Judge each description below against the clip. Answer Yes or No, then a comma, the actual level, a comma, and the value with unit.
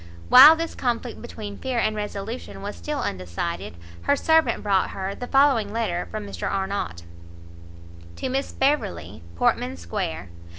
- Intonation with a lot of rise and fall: Yes, wide, 6.9 semitones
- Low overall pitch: No, high, 210 Hz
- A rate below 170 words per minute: Yes, average, 140 wpm